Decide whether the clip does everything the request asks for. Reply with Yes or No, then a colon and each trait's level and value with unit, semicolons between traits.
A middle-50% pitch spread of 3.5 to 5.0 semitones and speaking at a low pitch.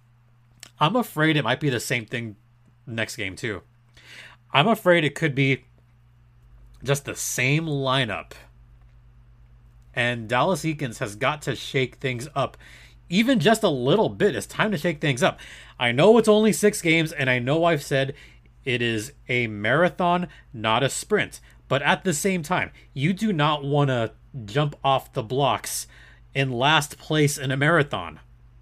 Yes: average, 4.7 semitones; low, 130 Hz